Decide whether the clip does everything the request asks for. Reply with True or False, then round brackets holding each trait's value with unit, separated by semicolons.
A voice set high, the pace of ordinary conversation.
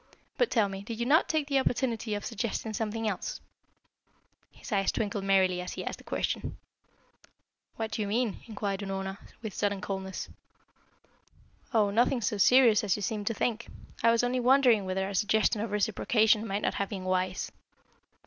True (210 Hz; 175 wpm)